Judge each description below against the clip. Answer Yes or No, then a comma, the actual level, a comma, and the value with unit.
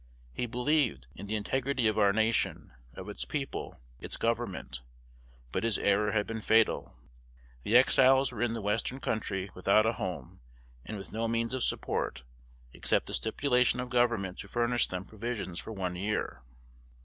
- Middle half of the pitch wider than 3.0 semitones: Yes, average, 3.4 semitones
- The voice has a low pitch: Yes, low, 110 Hz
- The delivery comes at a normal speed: Yes, average, 165 wpm